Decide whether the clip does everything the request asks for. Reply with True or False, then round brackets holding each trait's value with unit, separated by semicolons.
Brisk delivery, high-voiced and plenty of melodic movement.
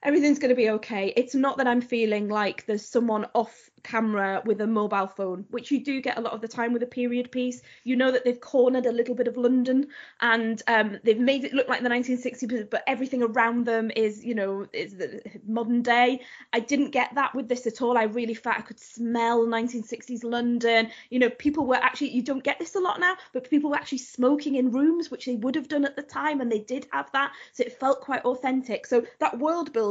False (235 wpm; 245 Hz; 2.5 semitones)